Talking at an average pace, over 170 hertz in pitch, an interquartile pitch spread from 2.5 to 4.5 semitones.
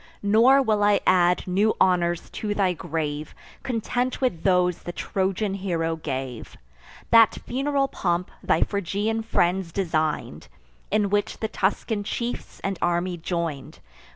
No: slow, 130 wpm; high, 190 Hz; average, 4.0 semitones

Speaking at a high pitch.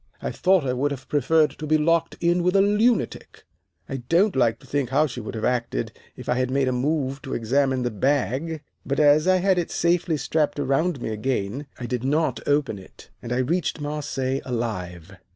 No: medium, 140 Hz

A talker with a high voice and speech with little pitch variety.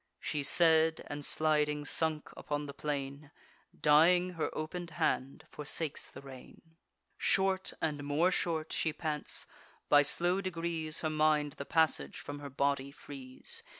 No: medium, 155 Hz; narrow, 2.1 semitones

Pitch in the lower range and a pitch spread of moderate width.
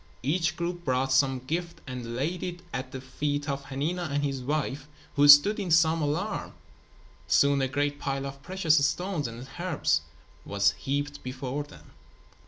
No: medium, 145 Hz; average, 3.6 semitones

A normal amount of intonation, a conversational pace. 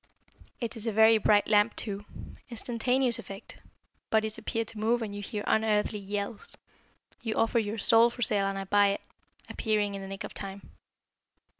No: narrow, 1.9 semitones; average, 175 wpm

